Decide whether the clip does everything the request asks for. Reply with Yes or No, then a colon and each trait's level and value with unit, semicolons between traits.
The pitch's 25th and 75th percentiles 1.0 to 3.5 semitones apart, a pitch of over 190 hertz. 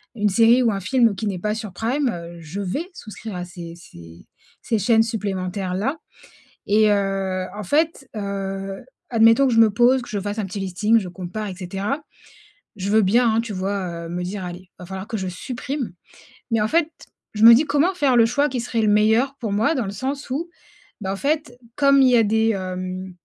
No: average, 4.2 semitones; high, 210 Hz